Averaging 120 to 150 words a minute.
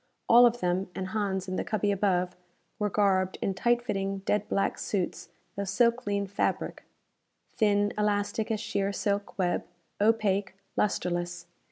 Yes: average, 145 wpm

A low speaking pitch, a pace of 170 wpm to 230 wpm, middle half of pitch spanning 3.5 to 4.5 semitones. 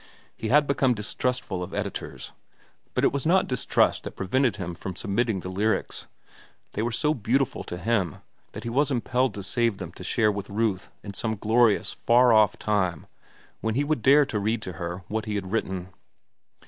Yes: low, 110 Hz; average, 190 wpm; average, 4.2 semitones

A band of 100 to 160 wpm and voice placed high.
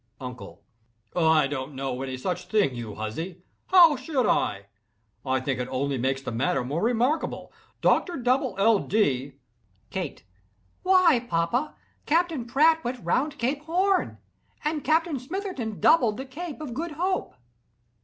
Yes: average, 145 wpm; high, 225 Hz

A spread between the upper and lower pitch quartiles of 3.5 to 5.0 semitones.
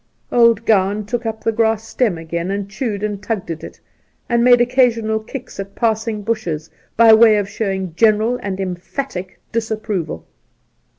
No: average, 2.8 semitones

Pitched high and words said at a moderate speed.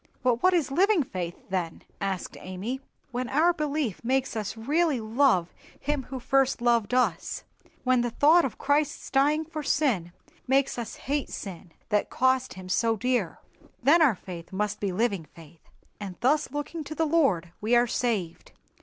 Yes: very high, 250 Hz; average, 165 wpm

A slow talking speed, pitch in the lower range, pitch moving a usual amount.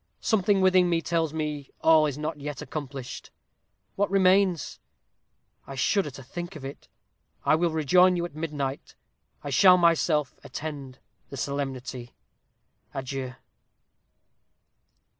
No: slow, 120 wpm; medium, 155 Hz; average, 4.1 semitones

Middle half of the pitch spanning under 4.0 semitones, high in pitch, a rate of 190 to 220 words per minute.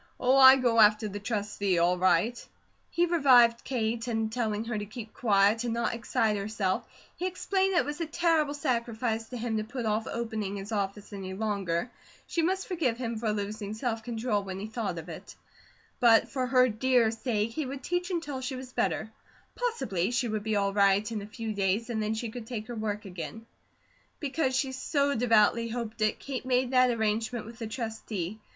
Yes: average, 3.3 semitones; high, 225 Hz; average, 200 wpm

